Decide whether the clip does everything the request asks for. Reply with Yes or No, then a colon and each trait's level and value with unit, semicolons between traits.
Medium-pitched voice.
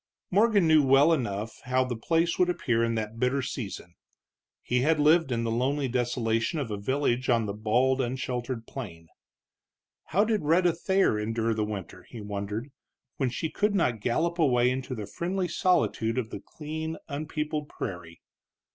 No: low, 130 Hz